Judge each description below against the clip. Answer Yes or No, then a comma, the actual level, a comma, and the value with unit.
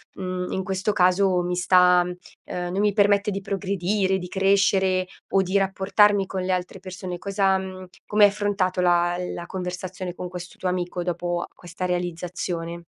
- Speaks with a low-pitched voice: No, medium, 185 Hz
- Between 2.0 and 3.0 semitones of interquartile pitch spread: No, narrow, 1.4 semitones